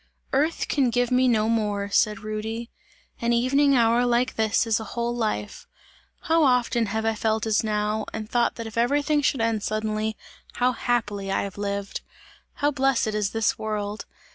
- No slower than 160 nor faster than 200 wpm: Yes, average, 175 wpm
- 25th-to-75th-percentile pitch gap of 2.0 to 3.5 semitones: Yes, narrow, 2.5 semitones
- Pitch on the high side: Yes, high, 225 Hz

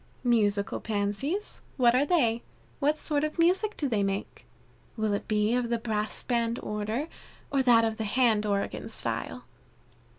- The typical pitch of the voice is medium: No, high, 230 Hz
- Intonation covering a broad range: No, average, 4.6 semitones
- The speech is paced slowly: No, average, 160 wpm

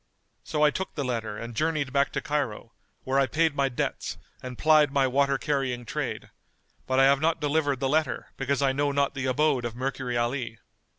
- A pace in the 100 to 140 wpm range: No, average, 200 wpm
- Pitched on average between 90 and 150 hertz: Yes, low, 135 Hz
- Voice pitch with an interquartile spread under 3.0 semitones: Yes, narrow, 2.5 semitones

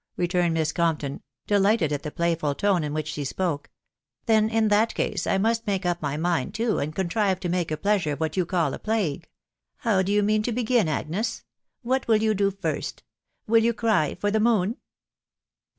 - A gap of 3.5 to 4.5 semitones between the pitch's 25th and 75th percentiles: No, average, 5.1 semitones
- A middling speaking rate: No, fast, 210 wpm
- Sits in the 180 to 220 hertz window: Yes, high, 190 Hz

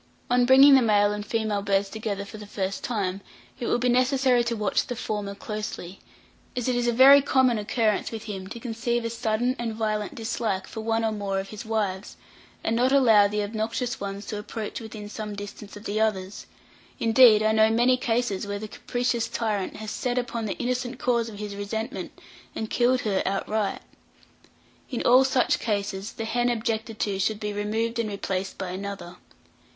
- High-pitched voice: Yes, high, 220 Hz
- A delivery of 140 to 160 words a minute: No, average, 190 wpm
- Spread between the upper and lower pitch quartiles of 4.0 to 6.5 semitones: No, average, 2.7 semitones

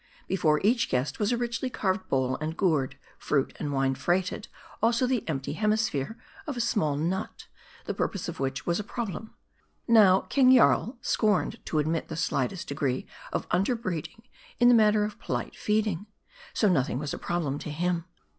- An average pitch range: No, wide, 6.7 semitones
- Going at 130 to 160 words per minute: No, average, 175 wpm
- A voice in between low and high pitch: Yes, medium, 180 Hz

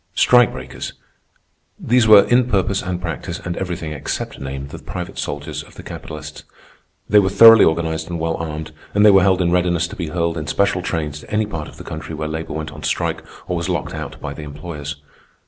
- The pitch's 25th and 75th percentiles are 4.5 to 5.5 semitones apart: No, average, 3.7 semitones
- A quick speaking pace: Yes, fast, 210 wpm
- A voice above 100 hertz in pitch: No, very low, 85 Hz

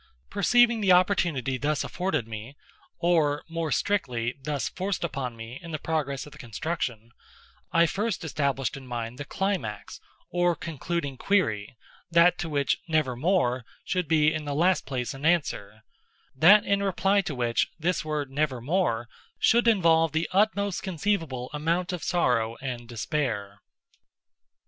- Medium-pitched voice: Yes, medium, 155 Hz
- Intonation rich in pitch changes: Yes, wide, 5.8 semitones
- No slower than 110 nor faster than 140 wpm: Yes, slow, 135 wpm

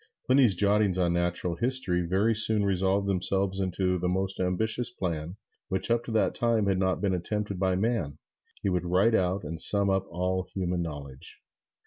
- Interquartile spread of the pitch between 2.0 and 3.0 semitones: Yes, narrow, 2.4 semitones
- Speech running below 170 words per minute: No, average, 175 wpm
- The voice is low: Yes, very low, 95 Hz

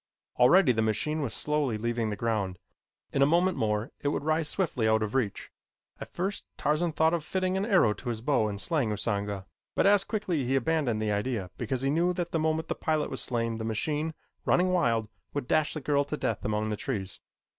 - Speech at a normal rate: No, fast, 215 wpm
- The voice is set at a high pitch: No, low, 135 Hz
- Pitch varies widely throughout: Yes, wide, 6.5 semitones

